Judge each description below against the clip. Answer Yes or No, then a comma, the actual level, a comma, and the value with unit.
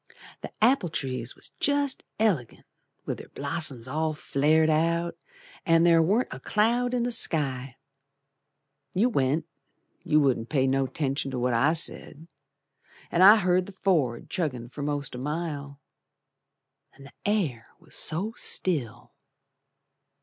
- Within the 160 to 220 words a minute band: No, slow, 135 wpm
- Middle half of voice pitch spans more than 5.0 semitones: Yes, wide, 5.4 semitones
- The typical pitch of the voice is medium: Yes, medium, 155 Hz